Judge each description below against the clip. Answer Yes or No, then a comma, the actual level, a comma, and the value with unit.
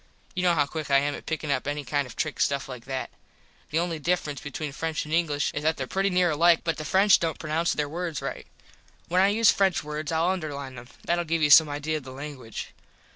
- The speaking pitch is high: No, medium, 155 Hz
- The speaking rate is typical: No, fast, 240 wpm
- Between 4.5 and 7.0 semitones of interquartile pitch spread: No, average, 3.0 semitones